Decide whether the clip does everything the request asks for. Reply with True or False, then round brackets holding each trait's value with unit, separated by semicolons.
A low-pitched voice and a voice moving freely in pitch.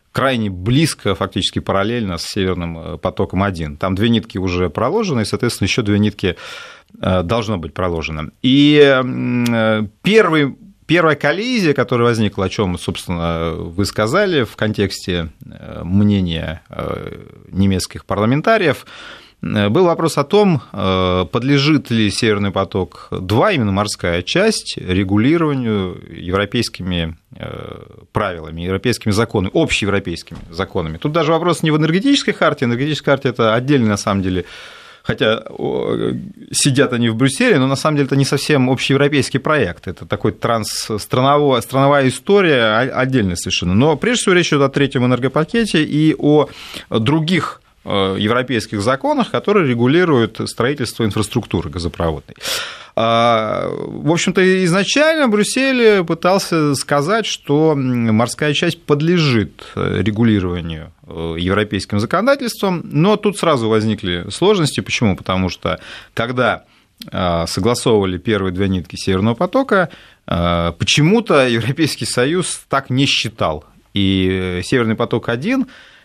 True (115 Hz; 7.3 semitones)